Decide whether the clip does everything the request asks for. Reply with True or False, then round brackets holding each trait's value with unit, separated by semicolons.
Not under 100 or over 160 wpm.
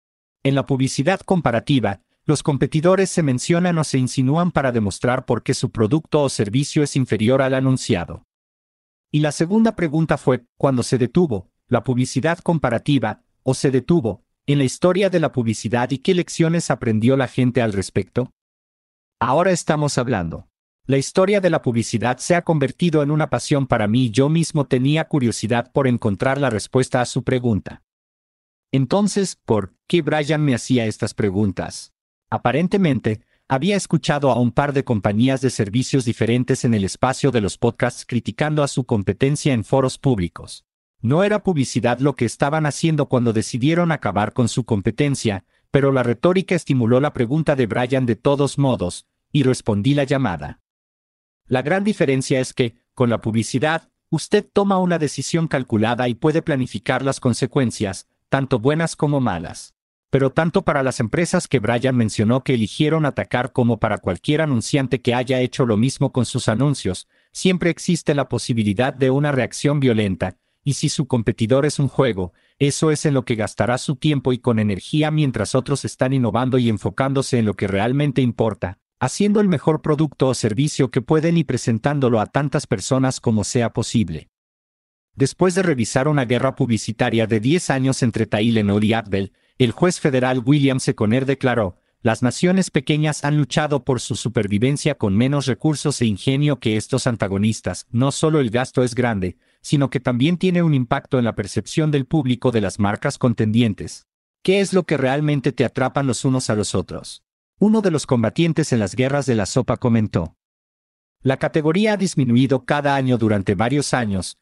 False (170 wpm)